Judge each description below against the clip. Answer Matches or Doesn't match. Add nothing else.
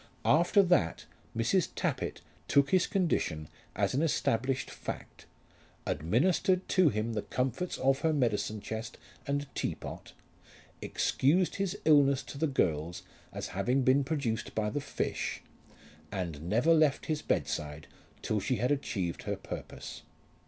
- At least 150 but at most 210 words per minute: Doesn't match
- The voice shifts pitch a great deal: Matches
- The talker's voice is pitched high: Doesn't match